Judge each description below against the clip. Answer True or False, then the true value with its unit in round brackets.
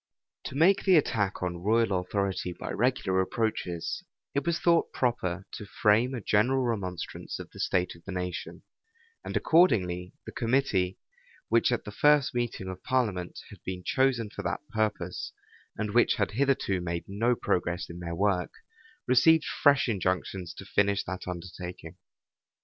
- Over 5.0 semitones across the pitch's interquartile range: True (5.4 semitones)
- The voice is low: True (105 Hz)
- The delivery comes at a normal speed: True (155 wpm)